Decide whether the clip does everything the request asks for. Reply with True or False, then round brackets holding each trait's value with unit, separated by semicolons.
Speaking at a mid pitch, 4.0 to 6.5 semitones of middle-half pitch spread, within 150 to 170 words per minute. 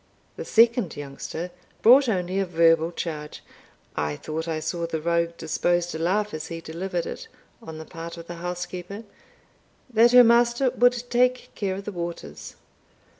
True (175 Hz; 4.8 semitones; 165 wpm)